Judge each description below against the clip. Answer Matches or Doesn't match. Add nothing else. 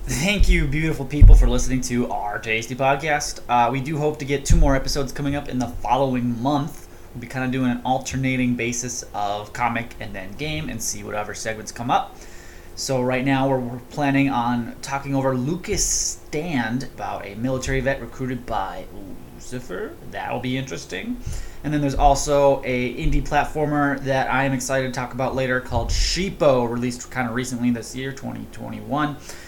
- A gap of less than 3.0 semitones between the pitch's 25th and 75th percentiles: Matches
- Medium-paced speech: Matches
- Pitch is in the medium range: Doesn't match